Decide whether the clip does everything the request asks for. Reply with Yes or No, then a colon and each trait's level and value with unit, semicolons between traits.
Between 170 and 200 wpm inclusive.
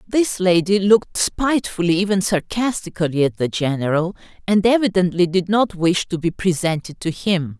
No: average, 150 wpm